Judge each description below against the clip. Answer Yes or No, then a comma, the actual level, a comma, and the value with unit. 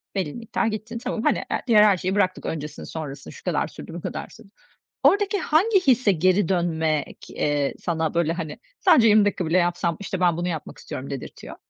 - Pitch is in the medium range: Yes, medium, 180 Hz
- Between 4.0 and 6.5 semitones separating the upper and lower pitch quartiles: Yes, average, 5.1 semitones